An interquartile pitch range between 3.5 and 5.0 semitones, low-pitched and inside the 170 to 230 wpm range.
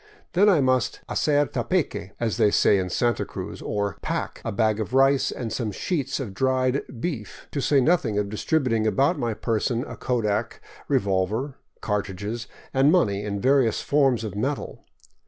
Yes: average, 4.7 semitones; low, 120 Hz; average, 180 wpm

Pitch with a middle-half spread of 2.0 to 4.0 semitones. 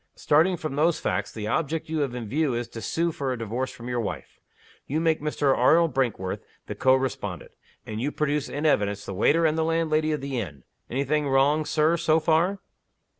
No: average, 4.5 semitones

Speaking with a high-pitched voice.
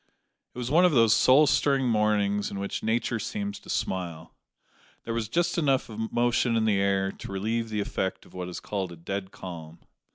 No: low, 110 Hz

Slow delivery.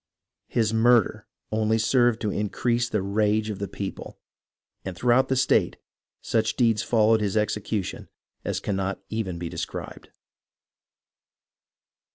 Yes: slow, 125 wpm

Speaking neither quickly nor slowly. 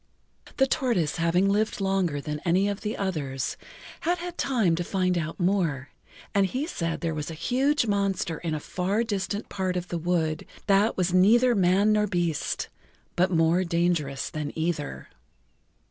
Yes: average, 165 wpm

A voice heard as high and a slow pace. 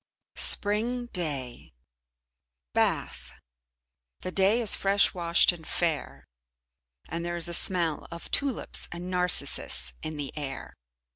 No: medium, 175 Hz; slow, 120 wpm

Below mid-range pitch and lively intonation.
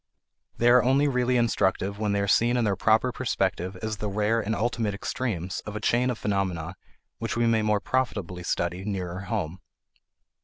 No: low, 105 Hz; average, 3.6 semitones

